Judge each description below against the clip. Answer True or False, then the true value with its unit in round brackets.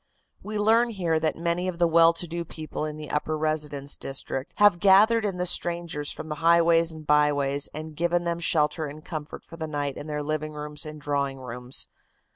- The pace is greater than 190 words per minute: True (205 wpm)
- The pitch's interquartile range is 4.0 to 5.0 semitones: False (2.4 semitones)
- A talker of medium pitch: True (155 Hz)